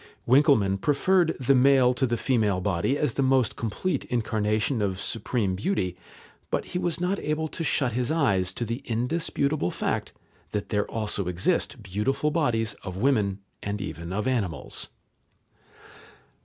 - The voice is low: Yes, low, 115 Hz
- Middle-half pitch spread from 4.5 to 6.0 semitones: Yes, wide, 5.6 semitones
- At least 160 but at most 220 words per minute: No, average, 150 wpm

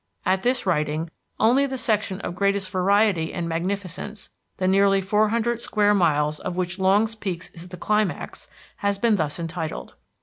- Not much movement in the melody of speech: No, average, 3.3 semitones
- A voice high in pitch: Yes, high, 195 Hz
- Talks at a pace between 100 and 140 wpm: No, average, 165 wpm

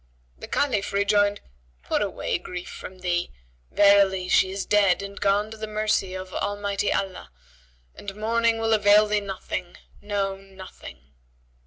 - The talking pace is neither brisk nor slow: Yes, average, 145 wpm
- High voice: Yes, high, 200 Hz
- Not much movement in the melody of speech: Yes, narrow, 1.7 semitones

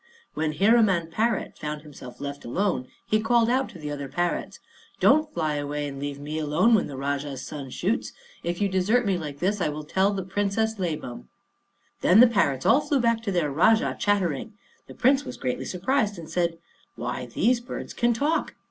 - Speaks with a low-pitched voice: No, medium, 180 Hz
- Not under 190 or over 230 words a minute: Yes, average, 195 wpm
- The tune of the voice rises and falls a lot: Yes, wide, 7.1 semitones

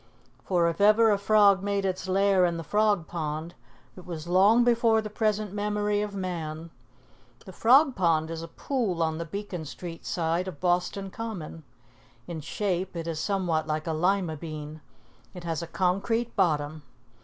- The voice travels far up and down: No, average, 3.9 semitones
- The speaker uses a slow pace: No, average, 170 wpm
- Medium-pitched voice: Yes, medium, 180 Hz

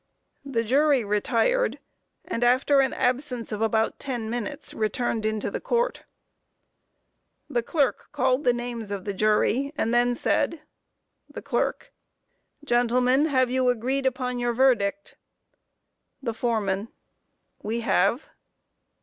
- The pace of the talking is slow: Yes, slow, 120 wpm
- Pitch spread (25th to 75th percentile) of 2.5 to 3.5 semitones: Yes, average, 2.9 semitones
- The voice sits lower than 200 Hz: No, high, 245 Hz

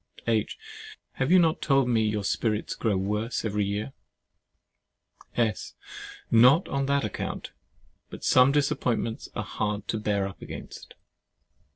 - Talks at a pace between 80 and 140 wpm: Yes, slow, 135 wpm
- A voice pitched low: Yes, low, 115 Hz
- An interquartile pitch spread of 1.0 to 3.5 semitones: No, average, 4.5 semitones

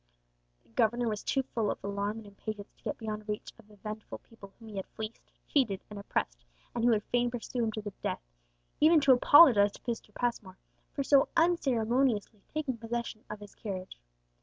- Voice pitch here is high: Yes, high, 220 Hz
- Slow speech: No, average, 195 wpm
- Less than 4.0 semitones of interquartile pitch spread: Yes, average, 2.9 semitones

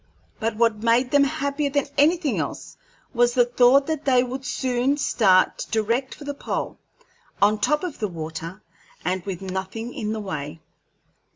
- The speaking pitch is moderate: No, high, 240 Hz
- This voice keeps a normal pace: Yes, average, 165 wpm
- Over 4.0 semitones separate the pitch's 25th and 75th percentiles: Yes, average, 5.2 semitones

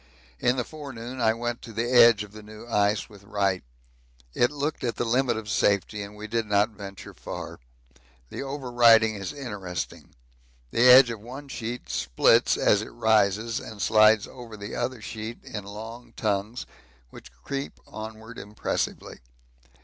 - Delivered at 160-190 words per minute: Yes, average, 165 wpm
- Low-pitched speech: Yes, low, 110 Hz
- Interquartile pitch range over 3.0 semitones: No, narrow, 2.5 semitones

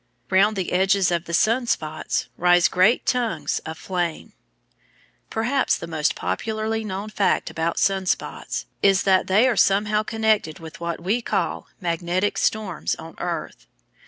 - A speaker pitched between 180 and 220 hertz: Yes, high, 190 Hz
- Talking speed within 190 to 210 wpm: No, average, 150 wpm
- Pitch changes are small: No, average, 4.0 semitones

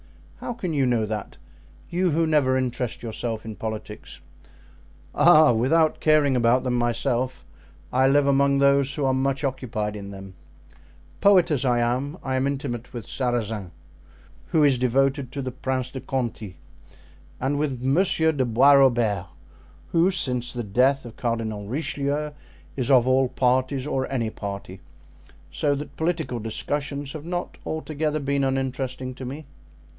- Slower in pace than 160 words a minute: Yes, average, 150 wpm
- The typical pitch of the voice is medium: No, low, 130 Hz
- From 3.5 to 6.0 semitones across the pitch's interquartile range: No, average, 3.0 semitones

